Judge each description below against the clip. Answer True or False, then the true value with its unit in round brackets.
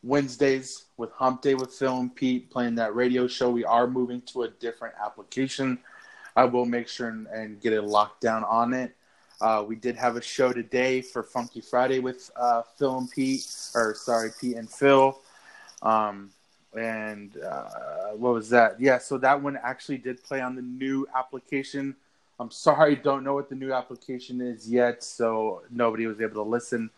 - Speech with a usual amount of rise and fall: False (2.3 semitones)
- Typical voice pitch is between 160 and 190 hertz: False (125 Hz)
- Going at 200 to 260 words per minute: False (185 wpm)